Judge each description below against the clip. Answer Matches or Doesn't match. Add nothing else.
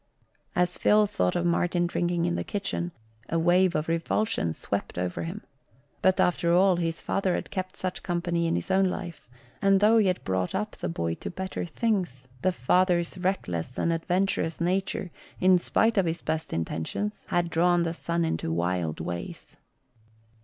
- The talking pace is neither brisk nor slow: Matches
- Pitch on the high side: Doesn't match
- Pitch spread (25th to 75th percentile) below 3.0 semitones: Matches